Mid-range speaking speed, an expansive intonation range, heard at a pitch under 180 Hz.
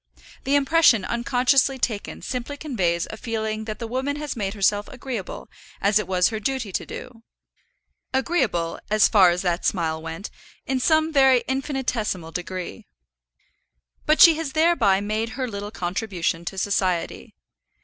No: average, 150 wpm; wide, 5.8 semitones; high, 220 Hz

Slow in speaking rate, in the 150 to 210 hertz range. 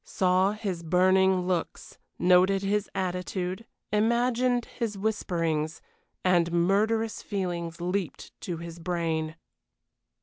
Yes: slow, 100 wpm; medium, 185 Hz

